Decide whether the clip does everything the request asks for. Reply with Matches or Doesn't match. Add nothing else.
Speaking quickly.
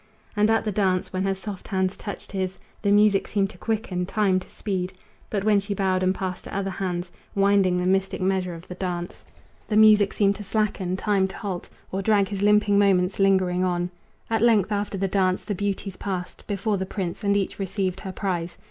Matches